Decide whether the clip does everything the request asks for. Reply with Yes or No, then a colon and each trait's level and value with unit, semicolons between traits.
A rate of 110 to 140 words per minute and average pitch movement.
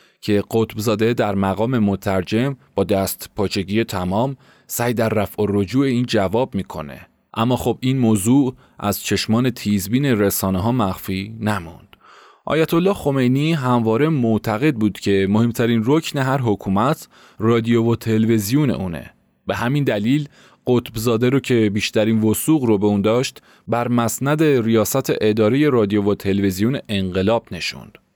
Yes: average, 135 wpm; average, 3.8 semitones